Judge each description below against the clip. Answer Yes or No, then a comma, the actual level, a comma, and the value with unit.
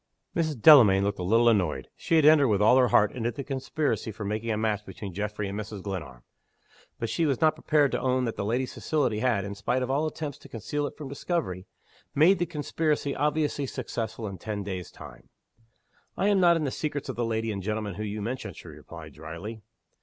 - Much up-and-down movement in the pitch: Yes, wide, 5.9 semitones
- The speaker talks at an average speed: No, fast, 220 wpm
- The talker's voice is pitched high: No, low, 115 Hz